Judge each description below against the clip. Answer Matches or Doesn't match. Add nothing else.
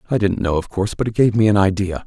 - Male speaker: Matches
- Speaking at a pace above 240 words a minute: Matches